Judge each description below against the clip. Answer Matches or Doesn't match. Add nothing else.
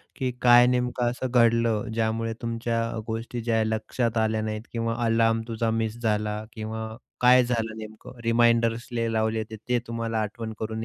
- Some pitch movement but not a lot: Doesn't match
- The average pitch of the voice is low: Matches